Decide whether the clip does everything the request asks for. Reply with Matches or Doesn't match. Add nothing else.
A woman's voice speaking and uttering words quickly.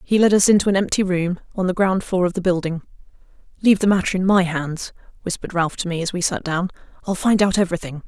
Matches